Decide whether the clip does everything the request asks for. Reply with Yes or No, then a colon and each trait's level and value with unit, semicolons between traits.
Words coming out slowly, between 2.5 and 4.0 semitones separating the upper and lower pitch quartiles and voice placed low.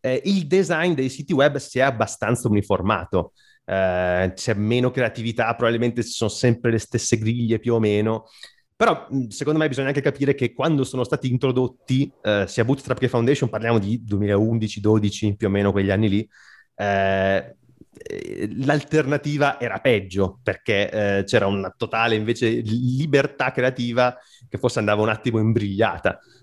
No: average, 150 wpm; average, 3.7 semitones; low, 120 Hz